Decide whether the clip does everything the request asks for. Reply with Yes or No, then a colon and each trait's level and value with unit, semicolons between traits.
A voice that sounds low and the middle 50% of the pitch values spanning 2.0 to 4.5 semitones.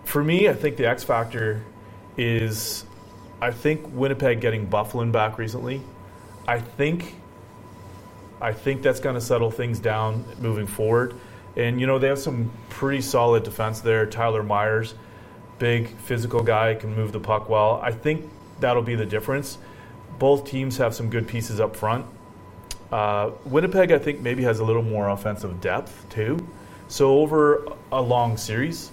Yes: low, 115 Hz; average, 3.0 semitones